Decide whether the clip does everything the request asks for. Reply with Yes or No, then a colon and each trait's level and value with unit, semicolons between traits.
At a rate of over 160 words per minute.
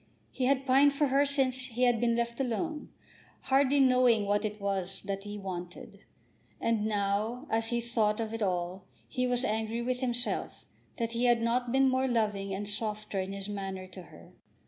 Yes: average, 190 wpm